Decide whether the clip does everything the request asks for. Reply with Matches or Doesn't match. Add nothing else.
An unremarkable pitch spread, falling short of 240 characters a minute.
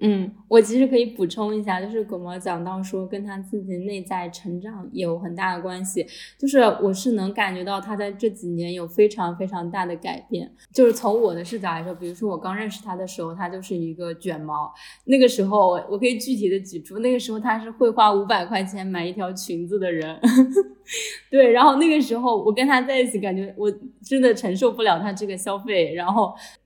Doesn't match